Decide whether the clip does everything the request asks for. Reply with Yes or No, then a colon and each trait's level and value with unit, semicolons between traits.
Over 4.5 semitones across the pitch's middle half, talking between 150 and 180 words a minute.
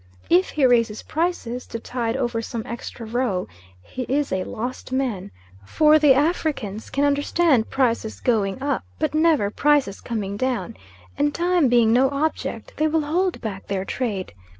Yes: average, 4.9 semitones; average, 160 wpm